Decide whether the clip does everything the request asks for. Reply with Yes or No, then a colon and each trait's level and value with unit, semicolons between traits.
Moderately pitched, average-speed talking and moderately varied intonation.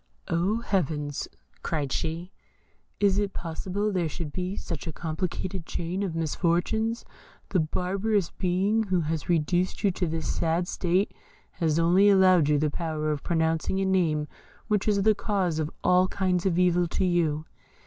Yes: medium, 175 Hz; average, 160 wpm; average, 3.0 semitones